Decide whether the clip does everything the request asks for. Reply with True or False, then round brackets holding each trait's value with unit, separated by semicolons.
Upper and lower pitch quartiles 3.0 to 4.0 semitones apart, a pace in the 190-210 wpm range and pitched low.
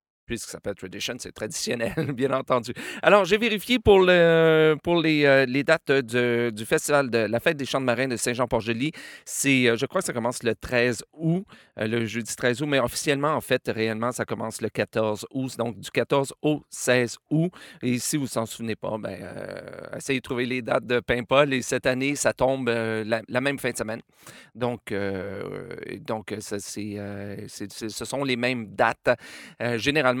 True (3.7 semitones; 205 wpm; 125 Hz)